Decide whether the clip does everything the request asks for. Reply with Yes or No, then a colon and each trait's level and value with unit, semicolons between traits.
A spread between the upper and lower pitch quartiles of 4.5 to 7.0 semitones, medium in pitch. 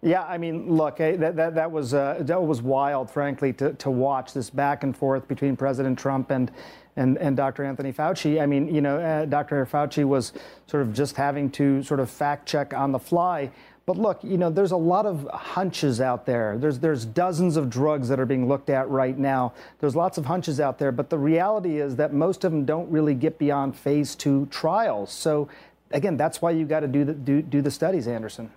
No: average, 2.7 semitones; medium, 145 Hz